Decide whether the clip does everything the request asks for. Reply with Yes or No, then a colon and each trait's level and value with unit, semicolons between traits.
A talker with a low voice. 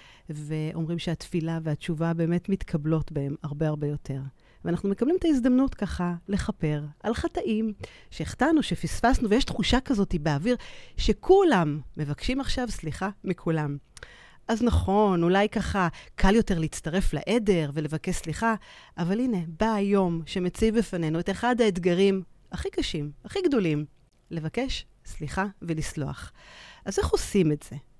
No: medium, 180 Hz